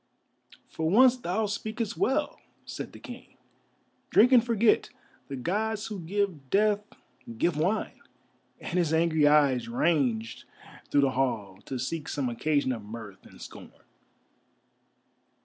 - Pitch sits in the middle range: Yes, medium, 160 Hz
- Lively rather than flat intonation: Yes, wide, 8.2 semitones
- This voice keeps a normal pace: No, slow, 130 wpm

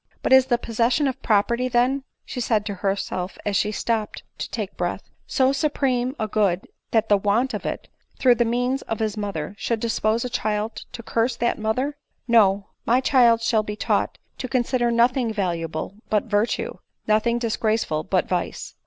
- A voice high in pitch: Yes, high, 230 Hz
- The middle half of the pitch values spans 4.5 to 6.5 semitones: No, average, 2.9 semitones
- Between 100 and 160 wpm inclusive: No, average, 185 wpm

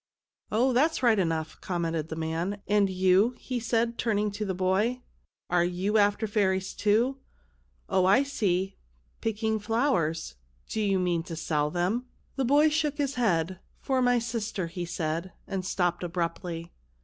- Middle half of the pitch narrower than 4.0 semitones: No, average, 4.8 semitones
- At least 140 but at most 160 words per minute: No, average, 175 wpm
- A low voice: No, high, 200 Hz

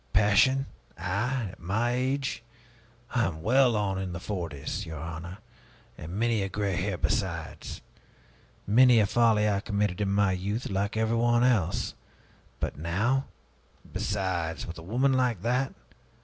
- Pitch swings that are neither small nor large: Yes, average, 4.5 semitones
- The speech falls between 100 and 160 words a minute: Yes, average, 145 wpm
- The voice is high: No, low, 105 Hz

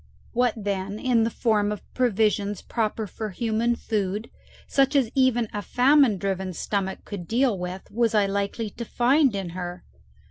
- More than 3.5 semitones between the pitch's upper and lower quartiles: No, average, 3.2 semitones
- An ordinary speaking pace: Yes, average, 165 wpm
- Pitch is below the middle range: No, high, 215 Hz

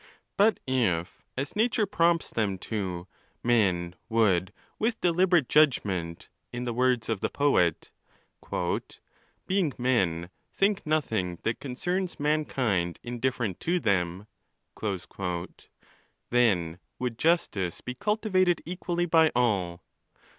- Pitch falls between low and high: No, low, 125 Hz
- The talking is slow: Yes, slow, 110 wpm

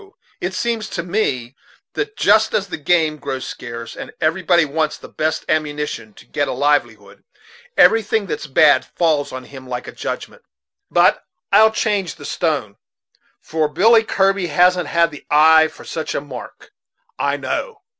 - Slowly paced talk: No, average, 160 wpm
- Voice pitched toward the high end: No, medium, 155 Hz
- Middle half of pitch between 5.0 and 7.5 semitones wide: Yes, average, 5.3 semitones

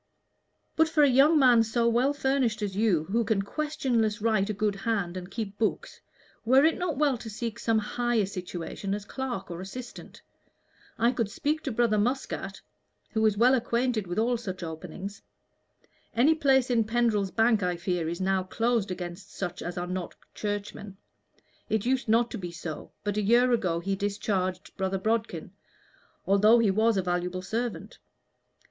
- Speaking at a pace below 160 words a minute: No, average, 175 wpm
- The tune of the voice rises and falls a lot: No, average, 3.9 semitones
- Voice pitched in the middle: No, high, 215 Hz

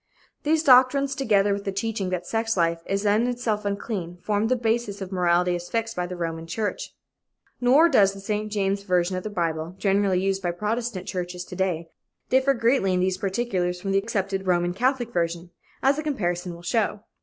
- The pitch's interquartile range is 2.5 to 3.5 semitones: No, average, 4.1 semitones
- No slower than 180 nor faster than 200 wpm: Yes, average, 195 wpm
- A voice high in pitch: Yes, high, 195 Hz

